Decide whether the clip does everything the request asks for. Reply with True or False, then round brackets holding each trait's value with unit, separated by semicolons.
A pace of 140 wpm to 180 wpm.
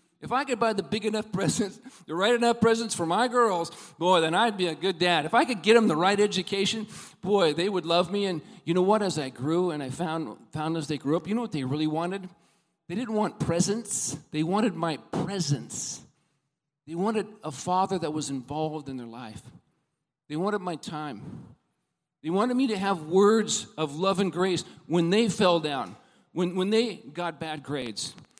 False (205 wpm)